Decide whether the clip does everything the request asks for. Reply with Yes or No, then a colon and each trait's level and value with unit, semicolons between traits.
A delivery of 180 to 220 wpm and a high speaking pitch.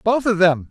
No: fast, 255 wpm; high, 195 Hz